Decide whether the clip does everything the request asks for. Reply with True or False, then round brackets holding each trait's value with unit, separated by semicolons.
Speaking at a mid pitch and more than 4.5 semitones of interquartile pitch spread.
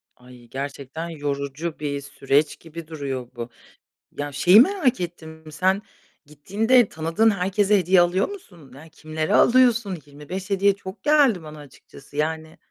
True (160 Hz; 5.2 semitones)